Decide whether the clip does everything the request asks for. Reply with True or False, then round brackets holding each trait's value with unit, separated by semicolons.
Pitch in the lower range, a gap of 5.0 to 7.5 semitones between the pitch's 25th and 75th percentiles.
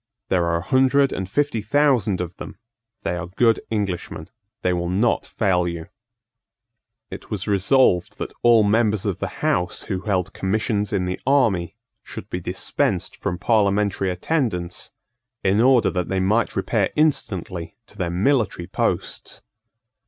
False (100 Hz; 4.3 semitones)